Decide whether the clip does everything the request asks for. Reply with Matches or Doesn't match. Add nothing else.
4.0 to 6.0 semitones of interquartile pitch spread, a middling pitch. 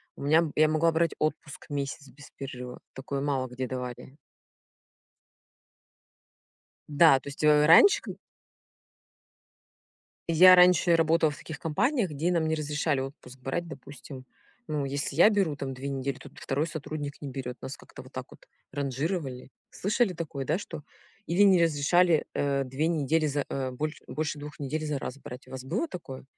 Doesn't match